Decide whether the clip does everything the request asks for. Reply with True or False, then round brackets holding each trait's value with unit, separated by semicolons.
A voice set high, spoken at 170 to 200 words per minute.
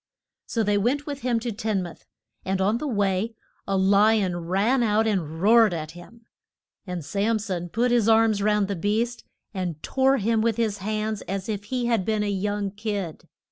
True (210 Hz; 195 wpm)